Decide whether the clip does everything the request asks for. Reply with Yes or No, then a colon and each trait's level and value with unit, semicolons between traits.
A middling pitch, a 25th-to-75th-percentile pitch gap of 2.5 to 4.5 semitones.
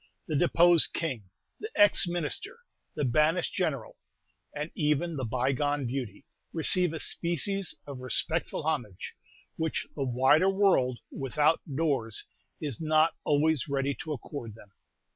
Yes: medium, 150 Hz; average, 4.0 semitones